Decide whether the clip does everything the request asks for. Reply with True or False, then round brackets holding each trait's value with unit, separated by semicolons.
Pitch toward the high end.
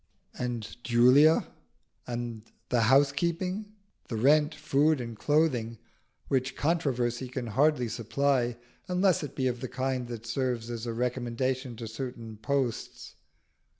False (125 Hz)